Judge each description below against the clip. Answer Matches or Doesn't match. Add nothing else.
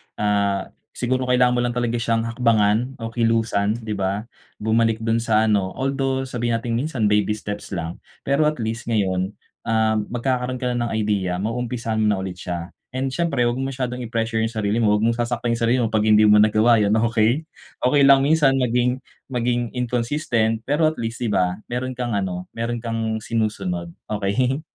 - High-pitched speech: Doesn't match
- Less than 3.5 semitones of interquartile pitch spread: Matches